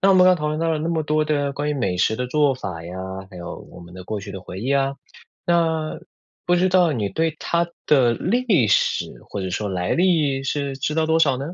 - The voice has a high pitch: No, medium, 145 Hz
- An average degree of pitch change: No, wide, 6.9 semitones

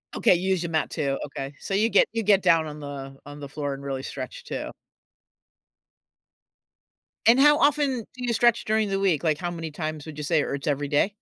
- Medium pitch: Yes, medium, 160 Hz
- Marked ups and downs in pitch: Yes, wide, 6.5 semitones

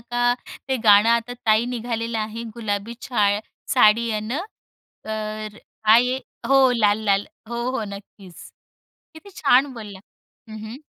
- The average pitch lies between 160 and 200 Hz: No, high, 225 Hz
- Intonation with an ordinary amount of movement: No, narrow, 2.3 semitones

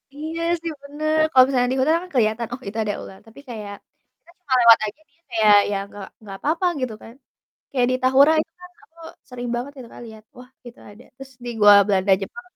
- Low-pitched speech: No, high, 245 Hz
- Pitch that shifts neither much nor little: Yes, average, 5.0 semitones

